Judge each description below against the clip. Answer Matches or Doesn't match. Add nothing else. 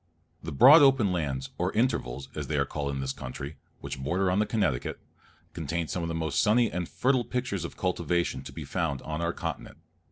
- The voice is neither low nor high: Doesn't match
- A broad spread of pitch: Matches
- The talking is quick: Matches